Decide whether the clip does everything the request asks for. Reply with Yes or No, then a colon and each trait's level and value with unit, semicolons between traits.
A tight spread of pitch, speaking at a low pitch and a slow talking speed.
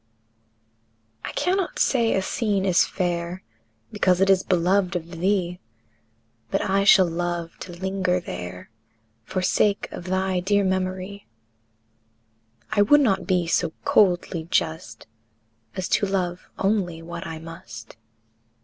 No: narrow, 2.2 semitones; medium, 185 Hz; slow, 130 wpm